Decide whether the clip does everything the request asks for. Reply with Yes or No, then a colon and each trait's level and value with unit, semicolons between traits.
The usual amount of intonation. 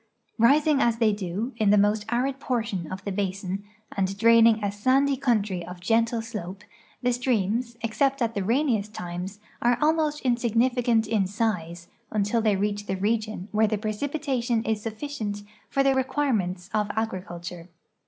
Yes: average, 3.4 semitones